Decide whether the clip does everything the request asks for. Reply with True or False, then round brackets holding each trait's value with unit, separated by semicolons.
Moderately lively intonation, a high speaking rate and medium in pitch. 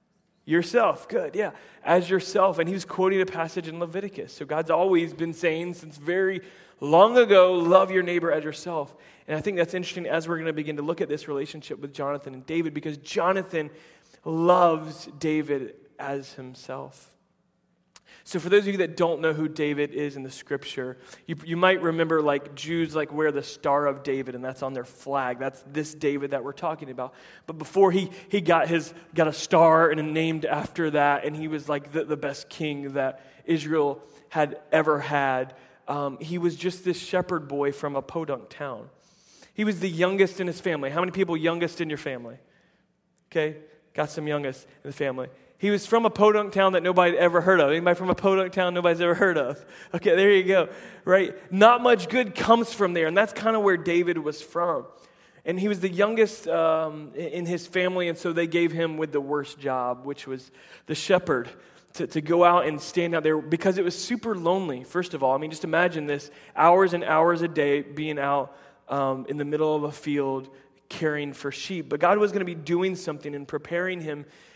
True (3.8 semitones; 210 wpm; 165 Hz)